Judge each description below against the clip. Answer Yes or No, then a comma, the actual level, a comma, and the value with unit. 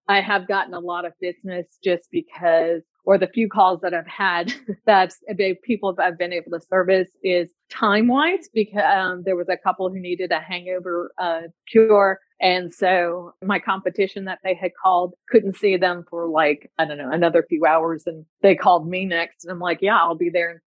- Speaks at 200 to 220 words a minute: Yes, fast, 205 wpm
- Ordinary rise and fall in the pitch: No, narrow, 2.2 semitones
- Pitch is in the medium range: Yes, medium, 180 Hz